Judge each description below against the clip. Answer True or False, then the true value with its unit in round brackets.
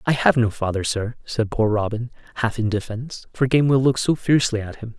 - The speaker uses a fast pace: True (215 wpm)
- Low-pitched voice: True (115 Hz)